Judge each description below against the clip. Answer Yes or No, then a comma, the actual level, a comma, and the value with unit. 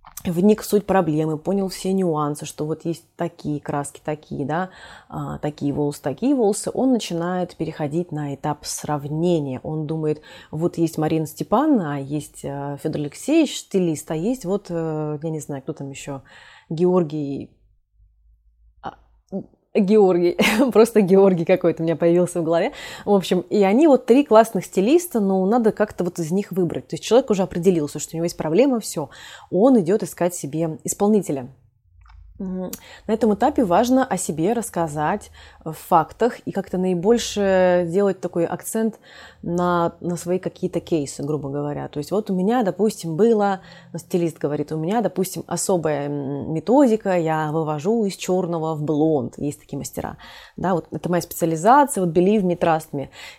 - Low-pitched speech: No, medium, 175 Hz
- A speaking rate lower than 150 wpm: No, average, 155 wpm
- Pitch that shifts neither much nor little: Yes, average, 4.3 semitones